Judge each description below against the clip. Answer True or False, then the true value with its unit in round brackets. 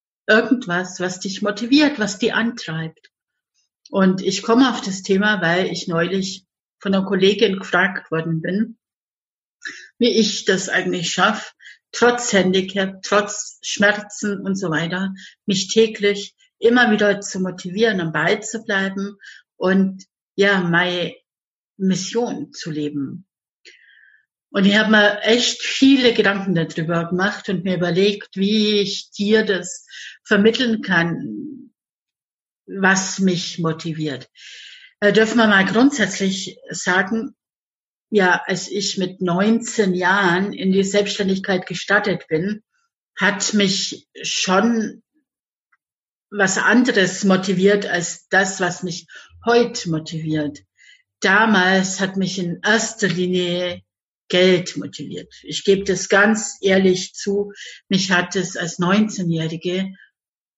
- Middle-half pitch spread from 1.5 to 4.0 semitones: True (2.9 semitones)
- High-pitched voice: True (195 Hz)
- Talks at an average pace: False (115 wpm)